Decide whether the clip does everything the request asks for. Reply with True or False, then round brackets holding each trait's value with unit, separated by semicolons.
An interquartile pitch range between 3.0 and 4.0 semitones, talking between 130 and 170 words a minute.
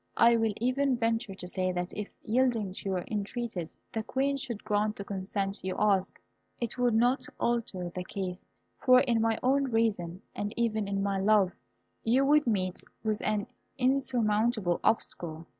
True (3.6 semitones; 165 wpm)